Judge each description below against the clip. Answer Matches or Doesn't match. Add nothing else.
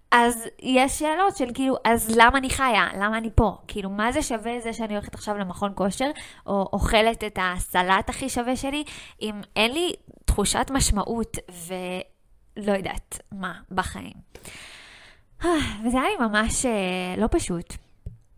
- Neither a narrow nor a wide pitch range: Matches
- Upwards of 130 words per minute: Matches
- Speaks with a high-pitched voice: Matches